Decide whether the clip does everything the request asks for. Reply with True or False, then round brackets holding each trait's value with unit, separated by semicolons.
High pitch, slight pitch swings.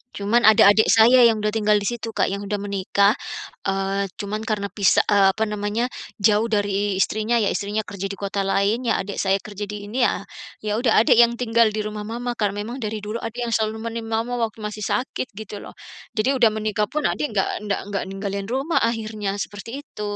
True (210 Hz; 2.0 semitones)